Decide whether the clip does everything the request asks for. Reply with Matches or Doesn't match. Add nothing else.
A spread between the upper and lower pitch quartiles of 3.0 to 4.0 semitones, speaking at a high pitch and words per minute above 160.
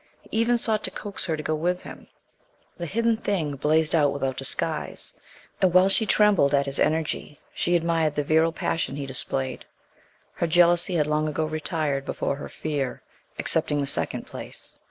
Doesn't match